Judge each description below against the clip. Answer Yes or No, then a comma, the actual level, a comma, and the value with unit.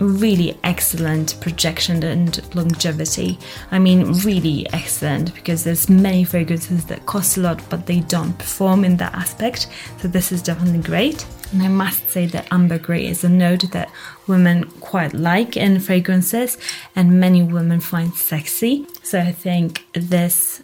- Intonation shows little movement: Yes, narrow, 1.7 semitones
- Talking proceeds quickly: No, average, 155 wpm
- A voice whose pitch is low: No, medium, 175 Hz